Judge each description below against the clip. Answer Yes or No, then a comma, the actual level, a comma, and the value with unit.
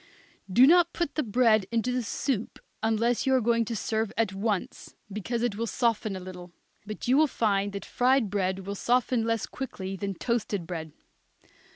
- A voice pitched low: No, high, 225 Hz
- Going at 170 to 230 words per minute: Yes, average, 185 wpm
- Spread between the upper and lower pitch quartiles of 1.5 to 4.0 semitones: Yes, average, 3.7 semitones